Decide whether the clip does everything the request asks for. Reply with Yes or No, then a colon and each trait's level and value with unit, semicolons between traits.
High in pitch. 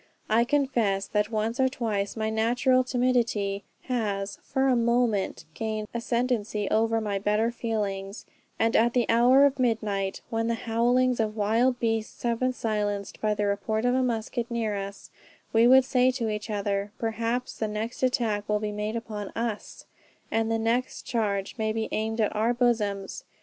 Yes: high, 225 Hz